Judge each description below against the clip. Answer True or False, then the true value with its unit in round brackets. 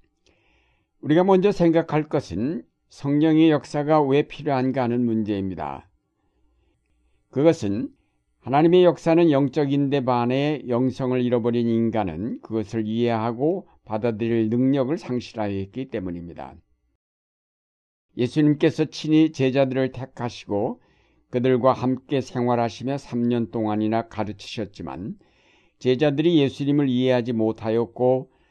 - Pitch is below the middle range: True (125 Hz)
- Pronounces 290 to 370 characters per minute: False (275 characters per minute)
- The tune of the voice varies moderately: True (4.8 semitones)